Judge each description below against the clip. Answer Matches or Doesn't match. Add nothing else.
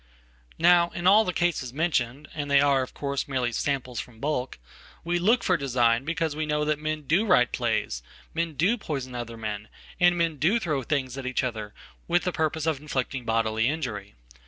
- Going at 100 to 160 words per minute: Doesn't match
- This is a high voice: Doesn't match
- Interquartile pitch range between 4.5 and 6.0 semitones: Matches